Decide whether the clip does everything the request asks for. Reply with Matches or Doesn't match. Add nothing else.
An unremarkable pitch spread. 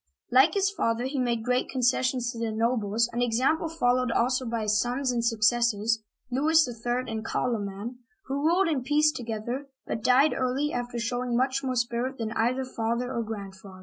Doesn't match